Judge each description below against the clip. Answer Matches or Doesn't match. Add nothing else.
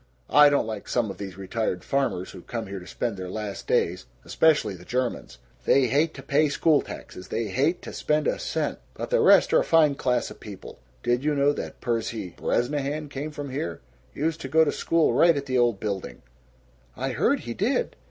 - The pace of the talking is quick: Matches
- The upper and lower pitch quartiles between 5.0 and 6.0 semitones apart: Matches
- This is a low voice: Matches